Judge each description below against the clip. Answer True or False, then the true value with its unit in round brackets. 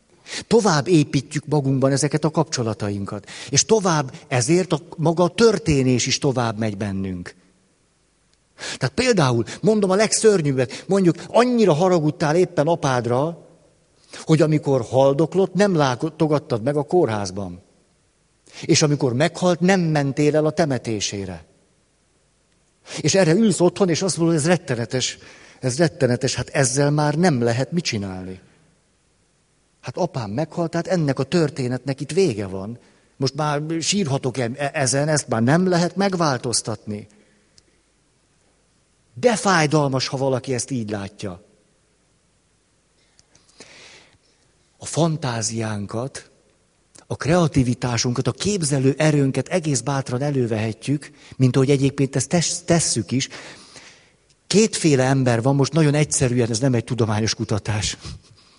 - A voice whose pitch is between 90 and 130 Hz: False (140 Hz)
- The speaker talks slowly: False (120 wpm)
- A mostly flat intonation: False (5.3 semitones)